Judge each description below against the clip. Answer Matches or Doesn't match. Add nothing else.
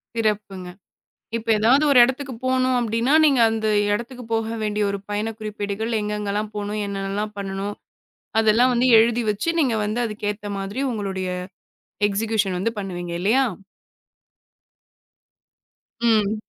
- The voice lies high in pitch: Matches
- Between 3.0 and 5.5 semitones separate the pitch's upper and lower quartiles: Doesn't match